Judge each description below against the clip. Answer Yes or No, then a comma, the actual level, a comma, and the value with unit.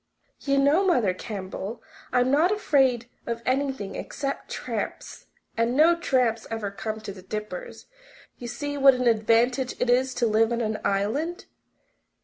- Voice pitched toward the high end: Yes, high, 245 Hz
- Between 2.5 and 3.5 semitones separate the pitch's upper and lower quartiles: No, average, 4.1 semitones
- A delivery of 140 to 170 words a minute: Yes, average, 150 wpm